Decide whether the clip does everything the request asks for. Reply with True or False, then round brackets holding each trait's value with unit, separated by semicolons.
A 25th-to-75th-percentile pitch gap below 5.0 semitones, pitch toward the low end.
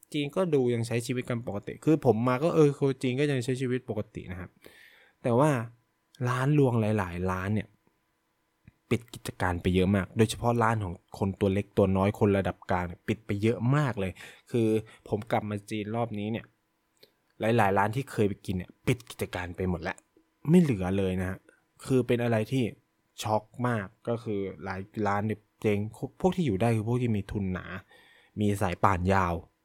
True (4.1 semitones; 110 Hz)